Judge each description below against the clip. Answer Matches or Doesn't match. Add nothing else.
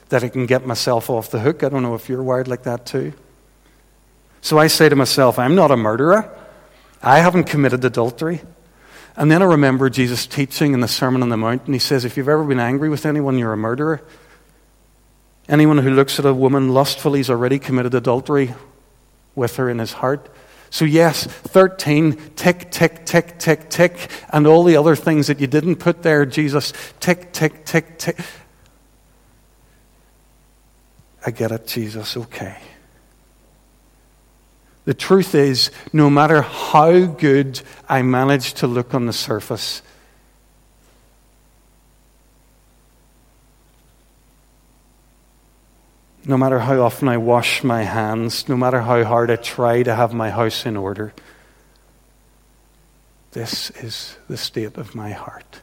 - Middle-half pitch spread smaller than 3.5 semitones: Doesn't match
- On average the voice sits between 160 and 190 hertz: Doesn't match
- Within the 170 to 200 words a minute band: Doesn't match